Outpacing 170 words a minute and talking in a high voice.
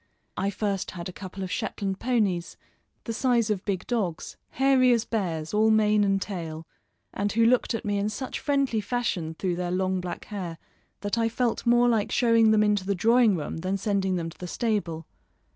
Yes: average, 195 wpm; high, 205 Hz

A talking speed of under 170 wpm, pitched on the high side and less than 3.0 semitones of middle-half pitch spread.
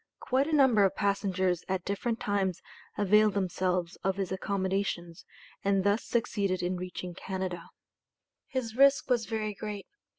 Yes: average, 140 wpm; high, 200 Hz; narrow, 2.6 semitones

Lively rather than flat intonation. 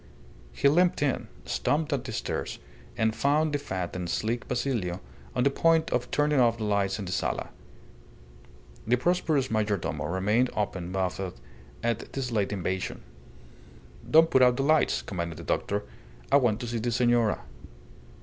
Yes: wide, 6.0 semitones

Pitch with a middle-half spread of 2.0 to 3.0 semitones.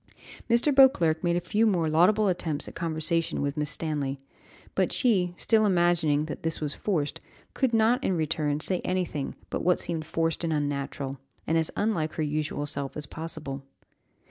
No: average, 3.5 semitones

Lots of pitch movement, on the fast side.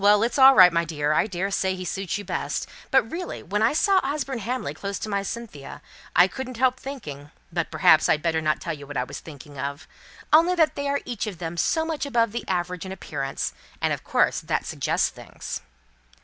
Yes: wide, 7.9 semitones; fast, 210 wpm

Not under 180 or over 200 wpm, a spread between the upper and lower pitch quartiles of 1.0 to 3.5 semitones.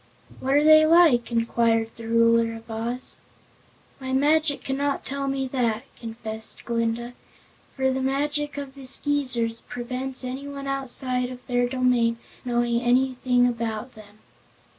No: slow, 135 wpm; average, 2.8 semitones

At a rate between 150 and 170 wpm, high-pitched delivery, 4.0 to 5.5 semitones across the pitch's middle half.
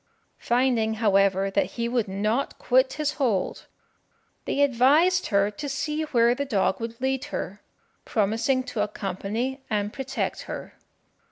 No: average, 140 wpm; high, 235 Hz; average, 4.4 semitones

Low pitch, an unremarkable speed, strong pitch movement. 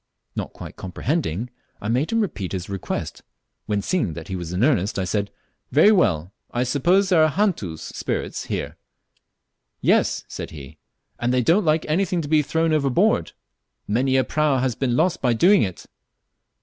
Yes: low, 130 Hz; average, 170 wpm; wide, 8.3 semitones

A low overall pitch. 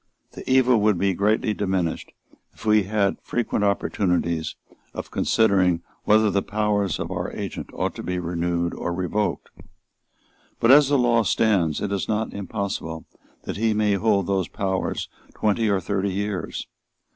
Yes: low, 100 Hz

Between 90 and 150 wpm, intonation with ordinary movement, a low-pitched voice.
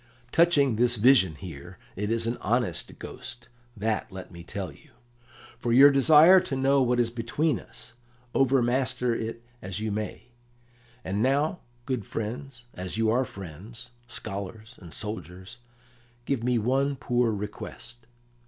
Yes: average, 145 wpm; average, 4.0 semitones; low, 120 Hz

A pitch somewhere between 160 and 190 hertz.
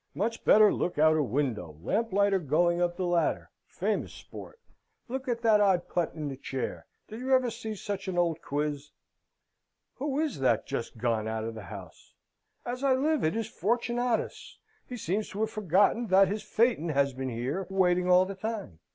Yes: medium, 185 Hz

